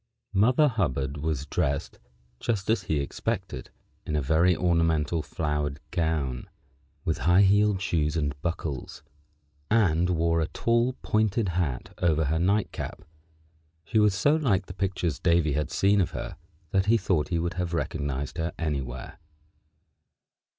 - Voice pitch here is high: No, very low, 85 Hz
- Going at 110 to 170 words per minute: Yes, average, 145 wpm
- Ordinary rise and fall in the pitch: Yes, average, 4.5 semitones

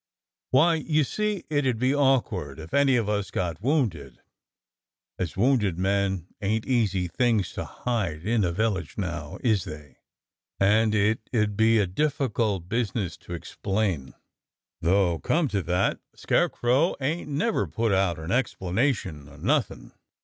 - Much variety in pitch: Yes, wide, 5.8 semitones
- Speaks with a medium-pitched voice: No, low, 105 Hz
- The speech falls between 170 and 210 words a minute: No, average, 150 wpm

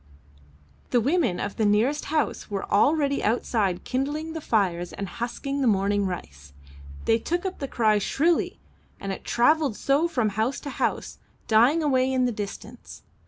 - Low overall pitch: No, high, 240 Hz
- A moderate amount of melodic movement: No, wide, 5.7 semitones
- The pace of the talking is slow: No, average, 165 wpm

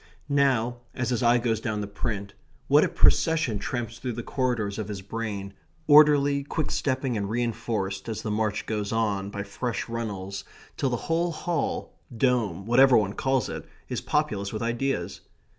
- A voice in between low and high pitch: No, low, 115 Hz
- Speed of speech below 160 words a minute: No, average, 170 wpm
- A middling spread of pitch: Yes, average, 4.2 semitones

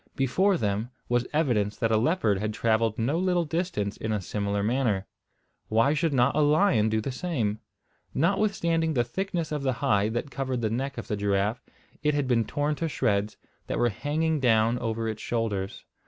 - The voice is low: Yes, low, 120 Hz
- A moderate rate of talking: Yes, average, 185 wpm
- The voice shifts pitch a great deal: Yes, wide, 5.8 semitones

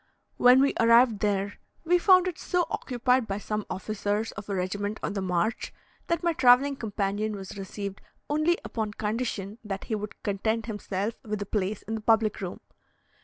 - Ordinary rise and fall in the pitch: Yes, average, 3.5 semitones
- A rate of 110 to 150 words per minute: No, average, 175 wpm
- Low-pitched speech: No, high, 215 Hz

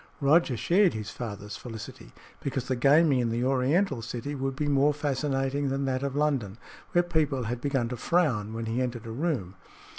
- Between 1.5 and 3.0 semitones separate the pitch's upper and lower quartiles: No, average, 3.7 semitones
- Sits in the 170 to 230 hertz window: No, low, 135 Hz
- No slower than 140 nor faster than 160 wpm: No, average, 185 wpm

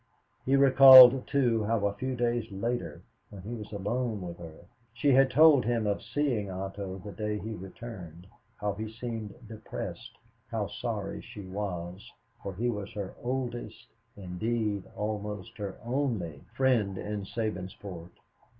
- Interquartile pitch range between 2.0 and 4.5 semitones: Yes, average, 3.6 semitones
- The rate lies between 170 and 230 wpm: No, average, 145 wpm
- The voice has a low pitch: Yes, low, 105 Hz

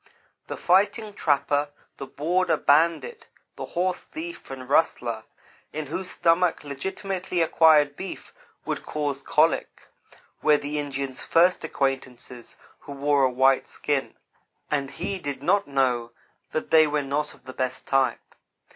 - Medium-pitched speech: Yes, medium, 145 Hz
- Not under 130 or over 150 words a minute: Yes, average, 140 wpm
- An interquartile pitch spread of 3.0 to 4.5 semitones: Yes, average, 3.9 semitones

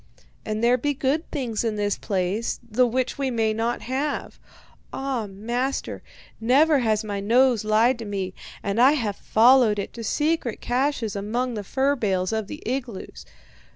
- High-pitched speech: Yes, high, 235 Hz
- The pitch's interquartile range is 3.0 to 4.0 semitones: Yes, average, 3.6 semitones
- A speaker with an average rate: Yes, average, 170 wpm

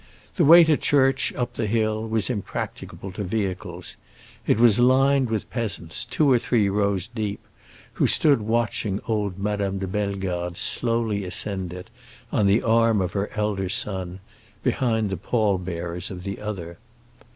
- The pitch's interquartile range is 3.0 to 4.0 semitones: Yes, average, 3.4 semitones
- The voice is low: Yes, low, 105 Hz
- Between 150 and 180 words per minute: Yes, average, 155 wpm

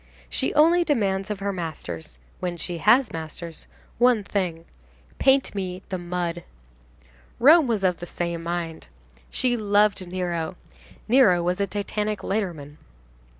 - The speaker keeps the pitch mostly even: No, average, 3.7 semitones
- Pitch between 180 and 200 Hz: Yes, medium, 185 Hz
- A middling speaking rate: No, slow, 125 wpm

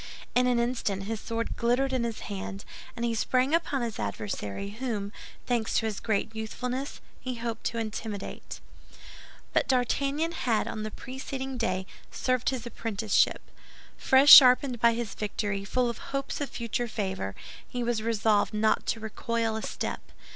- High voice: Yes, high, 230 Hz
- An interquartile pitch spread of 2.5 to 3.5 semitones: Yes, average, 2.9 semitones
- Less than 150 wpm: No, average, 160 wpm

